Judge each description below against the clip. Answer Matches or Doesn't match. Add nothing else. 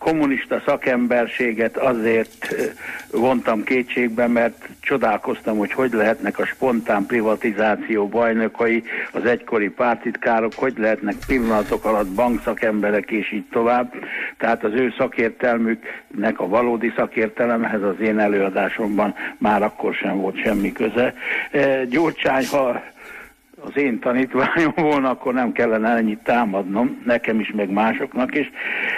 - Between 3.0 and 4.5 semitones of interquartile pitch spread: Doesn't match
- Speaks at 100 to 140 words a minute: Matches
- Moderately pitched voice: Doesn't match